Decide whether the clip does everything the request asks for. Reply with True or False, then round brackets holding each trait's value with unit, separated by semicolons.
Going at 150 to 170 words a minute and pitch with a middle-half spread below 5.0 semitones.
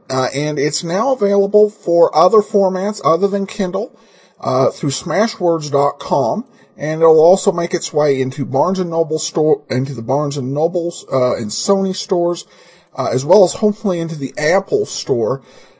False (155 wpm; 5.4 semitones)